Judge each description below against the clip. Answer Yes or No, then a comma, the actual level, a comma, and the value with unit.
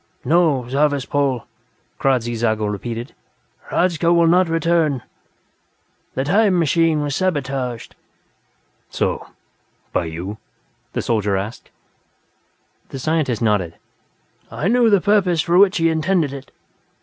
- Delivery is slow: Yes, slow, 115 wpm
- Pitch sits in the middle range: Yes, medium, 145 Hz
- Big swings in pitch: Yes, wide, 6.2 semitones